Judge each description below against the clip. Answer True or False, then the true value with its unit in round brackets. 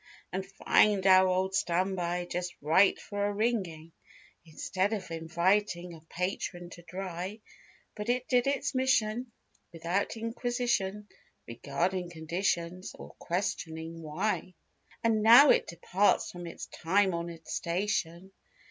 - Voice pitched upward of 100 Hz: True (185 Hz)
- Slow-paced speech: True (120 wpm)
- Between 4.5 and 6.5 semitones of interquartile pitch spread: False (3.5 semitones)